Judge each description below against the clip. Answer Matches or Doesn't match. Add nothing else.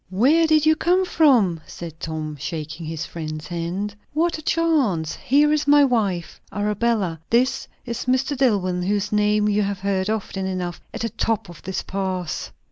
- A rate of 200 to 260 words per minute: Doesn't match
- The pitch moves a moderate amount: Doesn't match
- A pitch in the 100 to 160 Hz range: Doesn't match